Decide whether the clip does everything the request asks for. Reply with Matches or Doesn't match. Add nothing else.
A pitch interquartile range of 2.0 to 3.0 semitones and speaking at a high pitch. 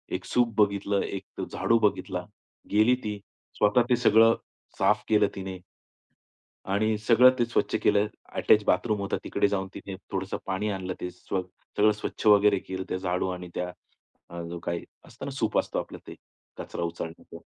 Doesn't match